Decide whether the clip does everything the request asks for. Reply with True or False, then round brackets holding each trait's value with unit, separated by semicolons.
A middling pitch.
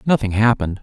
False (110 Hz)